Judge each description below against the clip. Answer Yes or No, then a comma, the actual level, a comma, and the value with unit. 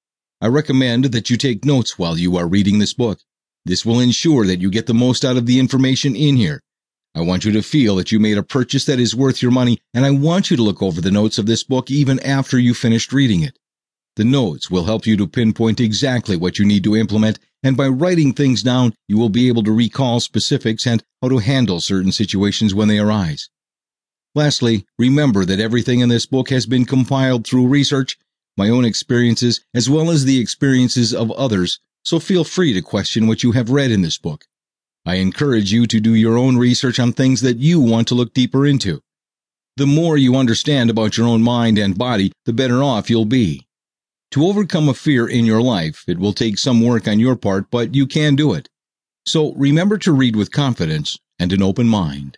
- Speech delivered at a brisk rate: Yes, fast, 215 wpm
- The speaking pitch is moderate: No, low, 120 Hz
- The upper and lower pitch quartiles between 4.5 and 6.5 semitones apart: No, average, 3.6 semitones